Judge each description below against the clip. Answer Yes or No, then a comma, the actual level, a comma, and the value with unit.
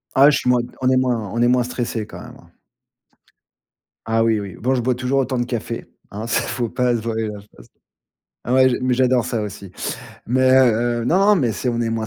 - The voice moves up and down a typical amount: No, narrow, 2.2 semitones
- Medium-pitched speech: No, low, 120 Hz